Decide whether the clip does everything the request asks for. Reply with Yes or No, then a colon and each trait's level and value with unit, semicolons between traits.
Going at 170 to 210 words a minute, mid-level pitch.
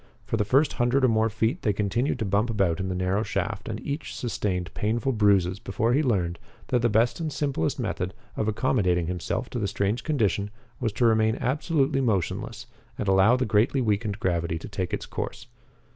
No: average, 195 wpm; low, 110 Hz